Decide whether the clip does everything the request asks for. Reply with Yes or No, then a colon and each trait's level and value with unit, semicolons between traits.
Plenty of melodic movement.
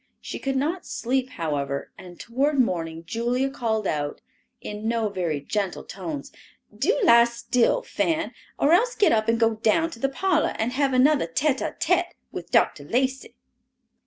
Yes: wide, 5.7 semitones